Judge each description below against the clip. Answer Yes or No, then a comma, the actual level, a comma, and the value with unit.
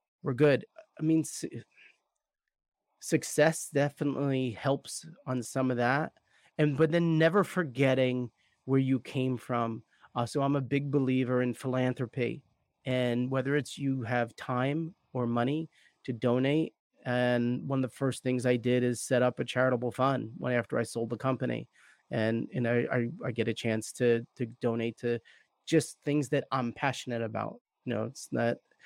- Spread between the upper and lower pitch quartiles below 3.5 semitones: Yes, average, 2.7 semitones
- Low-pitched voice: Yes, low, 130 Hz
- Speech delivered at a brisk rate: No, average, 170 wpm